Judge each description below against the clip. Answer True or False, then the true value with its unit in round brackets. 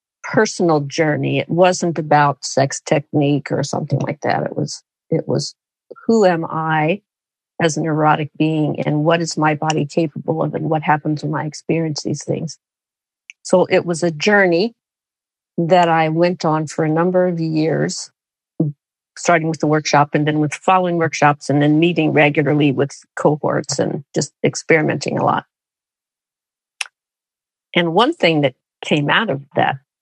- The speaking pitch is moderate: True (155 Hz)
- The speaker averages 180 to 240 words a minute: False (160 wpm)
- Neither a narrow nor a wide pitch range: False (2.2 semitones)